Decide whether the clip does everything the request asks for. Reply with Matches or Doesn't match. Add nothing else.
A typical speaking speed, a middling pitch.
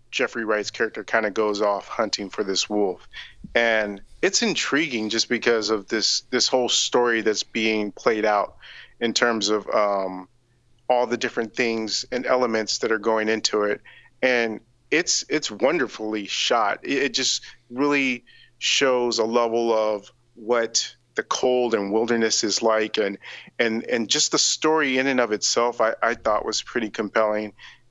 Doesn't match